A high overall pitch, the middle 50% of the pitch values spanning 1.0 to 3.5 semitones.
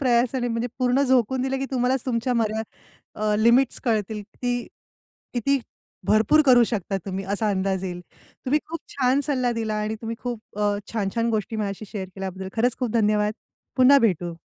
Yes: high, 230 Hz; average, 3.2 semitones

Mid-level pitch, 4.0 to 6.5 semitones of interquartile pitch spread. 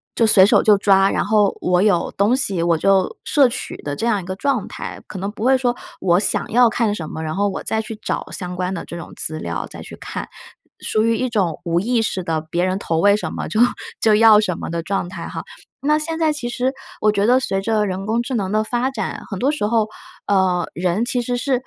No: high, 205 Hz; average, 4.4 semitones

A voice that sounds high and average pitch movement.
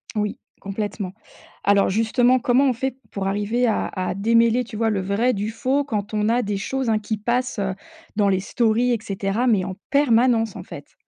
Yes: high, 220 Hz; average, 3.3 semitones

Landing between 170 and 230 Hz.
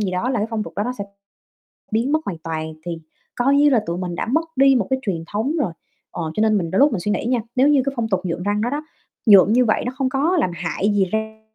Yes: high, 220 Hz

